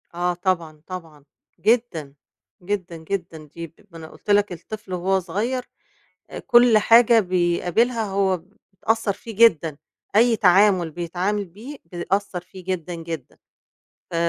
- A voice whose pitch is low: No, medium, 185 Hz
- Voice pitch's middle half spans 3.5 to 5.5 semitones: Yes, average, 3.8 semitones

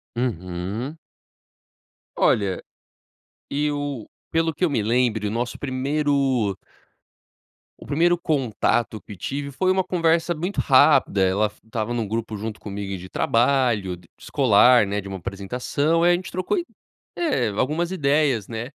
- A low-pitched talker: Yes, low, 125 Hz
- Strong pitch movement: Yes, wide, 6.3 semitones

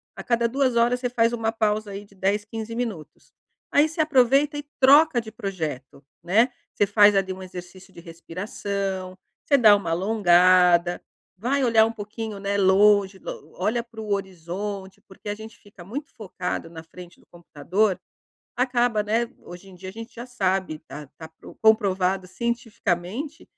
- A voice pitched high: Yes, high, 205 Hz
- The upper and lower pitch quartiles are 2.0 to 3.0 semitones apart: No, average, 4.0 semitones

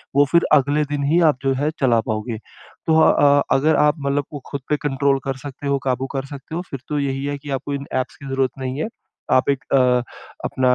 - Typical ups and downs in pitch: No, narrow, 1.5 semitones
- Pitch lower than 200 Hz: Yes, medium, 140 Hz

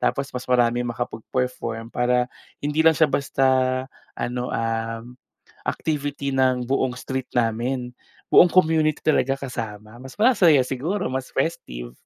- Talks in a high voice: No, low, 125 Hz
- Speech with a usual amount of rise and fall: Yes, average, 3.0 semitones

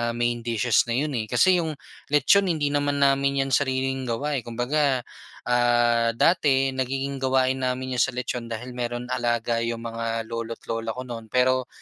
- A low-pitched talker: Yes, low, 125 Hz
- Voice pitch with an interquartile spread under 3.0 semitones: Yes, narrow, 2.5 semitones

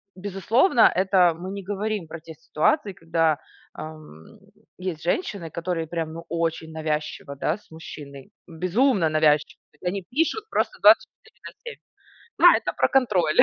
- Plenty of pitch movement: No, average, 4.1 semitones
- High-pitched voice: No, medium, 170 Hz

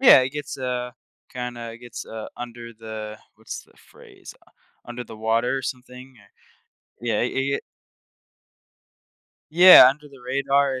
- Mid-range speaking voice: No, low, 125 Hz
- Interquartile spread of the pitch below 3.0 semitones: Yes, narrow, 2.4 semitones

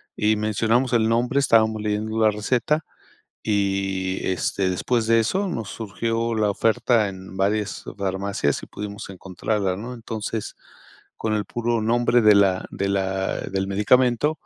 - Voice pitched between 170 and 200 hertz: No, low, 110 Hz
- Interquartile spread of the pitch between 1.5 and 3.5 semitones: Yes, average, 2.9 semitones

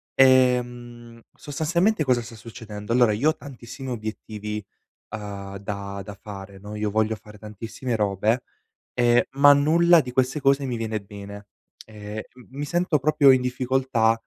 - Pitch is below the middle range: Yes, low, 120 Hz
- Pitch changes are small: No, average, 4.0 semitones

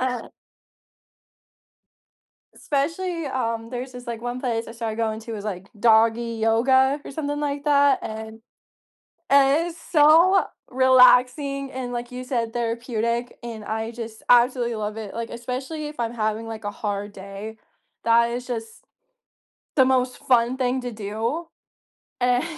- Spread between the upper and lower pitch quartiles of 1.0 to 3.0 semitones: Yes, average, 2.7 semitones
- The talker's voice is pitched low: No, high, 240 Hz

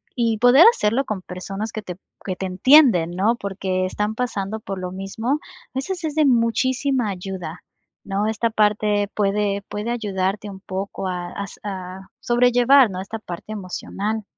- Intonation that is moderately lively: Yes, average, 3.6 semitones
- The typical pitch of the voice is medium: No, high, 210 Hz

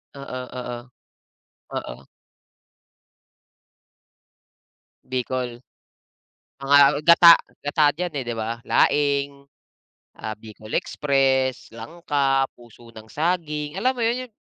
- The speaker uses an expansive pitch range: No, average, 3.8 semitones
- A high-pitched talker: No, medium, 140 Hz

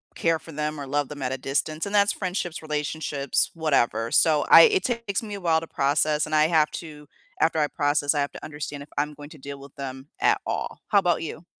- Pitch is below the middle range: No, medium, 150 Hz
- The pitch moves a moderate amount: No, narrow, 2.3 semitones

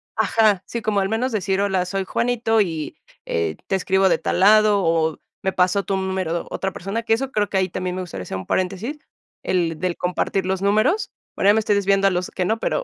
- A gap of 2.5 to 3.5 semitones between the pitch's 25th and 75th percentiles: Yes, average, 2.9 semitones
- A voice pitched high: Yes, high, 195 Hz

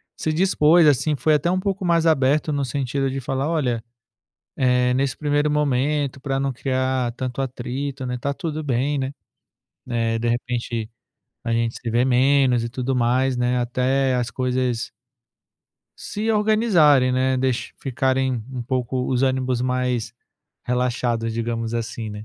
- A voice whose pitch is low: Yes, low, 130 Hz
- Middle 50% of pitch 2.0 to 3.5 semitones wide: Yes, narrow, 2.5 semitones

